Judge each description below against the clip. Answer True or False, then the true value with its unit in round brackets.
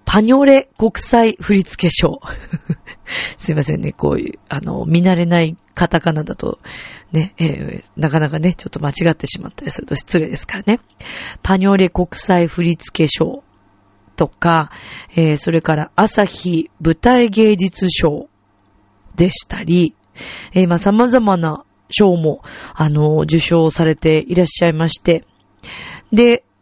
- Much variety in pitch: False (3.3 semitones)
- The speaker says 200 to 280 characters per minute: True (265 characters per minute)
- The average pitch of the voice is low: False (170 Hz)